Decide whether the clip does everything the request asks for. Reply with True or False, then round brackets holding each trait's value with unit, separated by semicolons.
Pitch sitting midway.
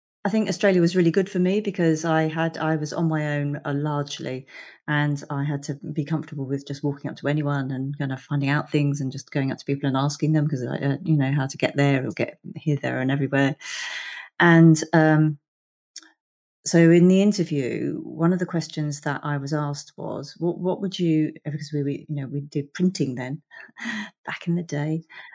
True (150 Hz)